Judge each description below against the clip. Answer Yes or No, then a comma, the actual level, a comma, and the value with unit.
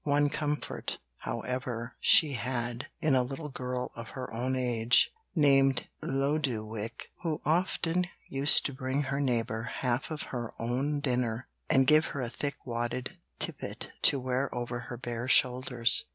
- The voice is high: No, low, 130 Hz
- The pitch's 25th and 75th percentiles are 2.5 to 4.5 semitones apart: Yes, average, 2.9 semitones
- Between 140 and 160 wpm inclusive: Yes, average, 150 wpm